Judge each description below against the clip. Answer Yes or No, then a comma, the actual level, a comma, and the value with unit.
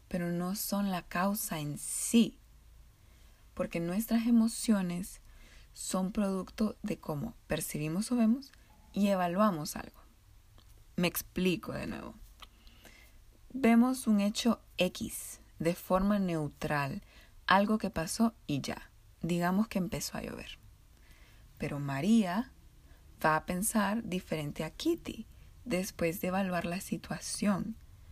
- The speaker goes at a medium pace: No, slow, 115 wpm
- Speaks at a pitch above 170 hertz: Yes, medium, 185 Hz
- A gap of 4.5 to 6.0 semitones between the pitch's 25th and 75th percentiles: Yes, wide, 5.6 semitones